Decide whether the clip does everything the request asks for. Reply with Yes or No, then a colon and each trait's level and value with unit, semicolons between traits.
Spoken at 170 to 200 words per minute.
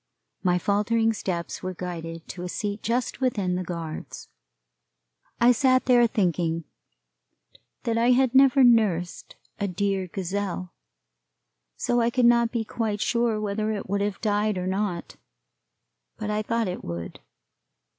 No: average, 145 wpm